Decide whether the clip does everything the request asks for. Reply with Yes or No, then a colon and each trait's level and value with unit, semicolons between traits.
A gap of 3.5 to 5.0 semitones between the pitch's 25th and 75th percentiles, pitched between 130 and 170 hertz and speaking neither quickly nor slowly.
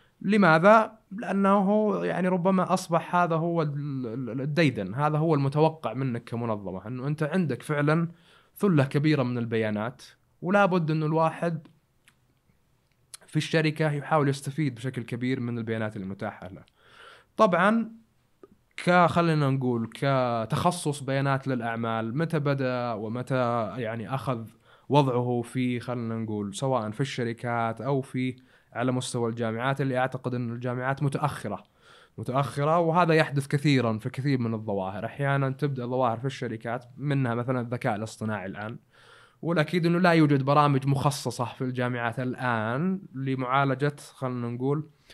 Yes: average, 4.4 semitones; low, 135 Hz; average, 125 wpm